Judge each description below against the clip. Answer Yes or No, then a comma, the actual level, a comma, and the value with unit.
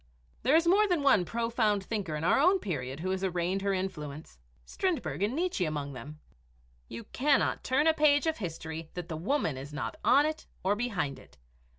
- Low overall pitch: No, high, 195 Hz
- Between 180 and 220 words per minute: Yes, average, 195 wpm